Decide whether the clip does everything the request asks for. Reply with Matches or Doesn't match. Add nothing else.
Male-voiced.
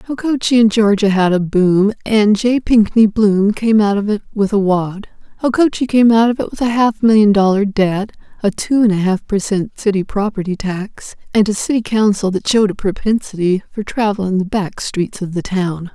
Doesn't match